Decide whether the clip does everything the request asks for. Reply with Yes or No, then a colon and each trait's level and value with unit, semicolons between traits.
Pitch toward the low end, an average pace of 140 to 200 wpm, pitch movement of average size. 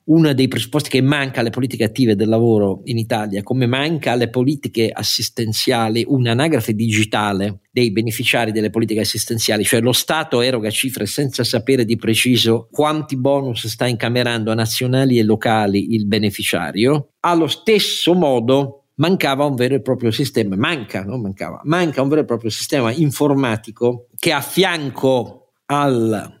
Yes: low, 120 Hz; average, 150 wpm; average, 3.7 semitones